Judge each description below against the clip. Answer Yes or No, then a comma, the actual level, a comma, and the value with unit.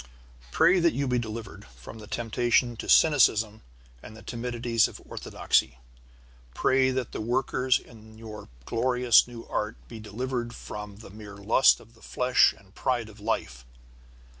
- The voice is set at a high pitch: No, low, 115 Hz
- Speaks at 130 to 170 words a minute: Yes, average, 160 wpm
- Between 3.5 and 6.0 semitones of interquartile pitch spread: No, narrow, 2.6 semitones